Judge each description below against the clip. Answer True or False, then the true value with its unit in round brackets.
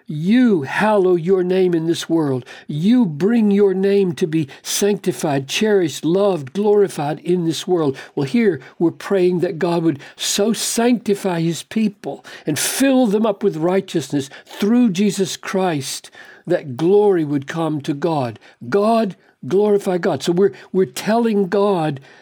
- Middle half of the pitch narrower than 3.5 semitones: False (3.8 semitones)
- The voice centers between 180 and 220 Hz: True (185 Hz)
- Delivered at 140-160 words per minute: True (145 wpm)